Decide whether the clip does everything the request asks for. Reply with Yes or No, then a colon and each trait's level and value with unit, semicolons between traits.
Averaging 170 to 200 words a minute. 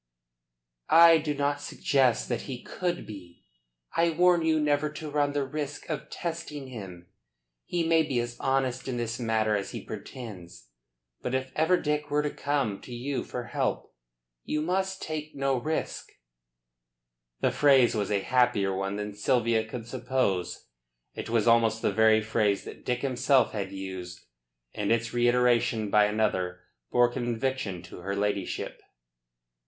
No: average, 155 wpm